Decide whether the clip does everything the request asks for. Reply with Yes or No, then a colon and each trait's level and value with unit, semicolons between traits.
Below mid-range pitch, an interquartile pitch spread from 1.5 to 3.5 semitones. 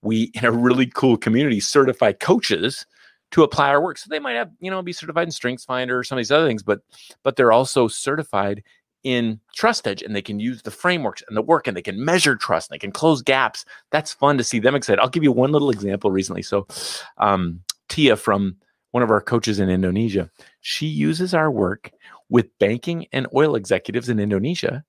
No: low, 120 Hz; wide, 5.4 semitones